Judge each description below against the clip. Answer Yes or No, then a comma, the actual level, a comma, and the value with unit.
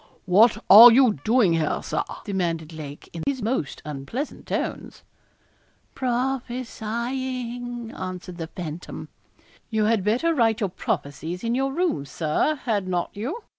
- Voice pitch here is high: Yes, high, 220 Hz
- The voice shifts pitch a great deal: Yes, wide, 6.1 semitones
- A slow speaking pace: Yes, slow, 130 wpm